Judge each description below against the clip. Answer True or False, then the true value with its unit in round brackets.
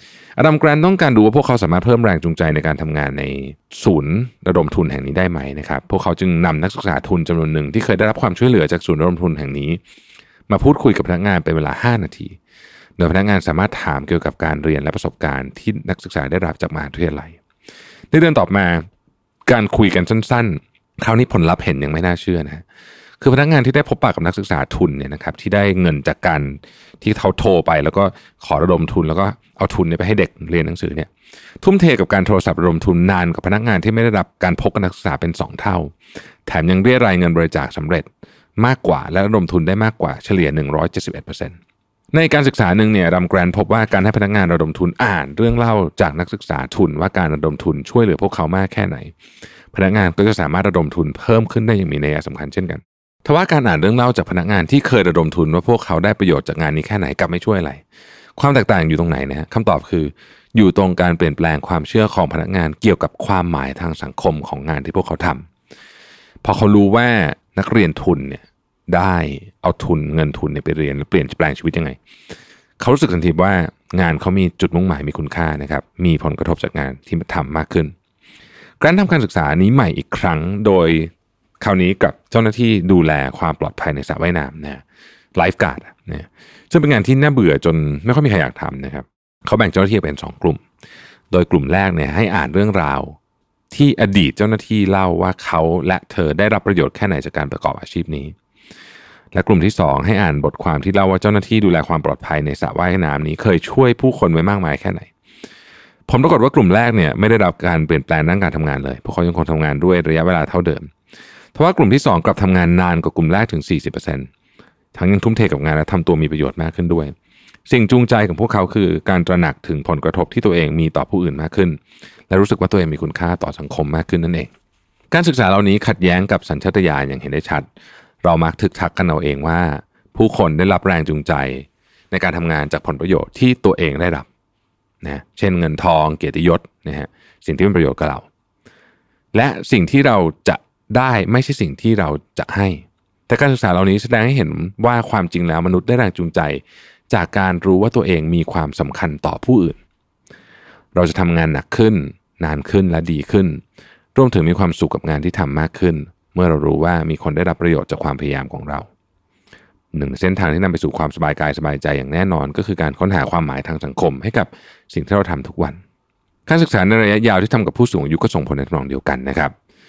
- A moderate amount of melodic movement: True (4.6 semitones)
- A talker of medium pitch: False (90 Hz)